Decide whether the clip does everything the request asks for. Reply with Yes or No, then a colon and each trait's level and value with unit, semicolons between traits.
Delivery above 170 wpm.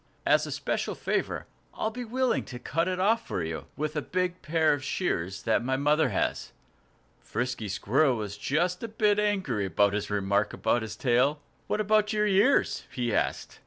Yes: average, 185 wpm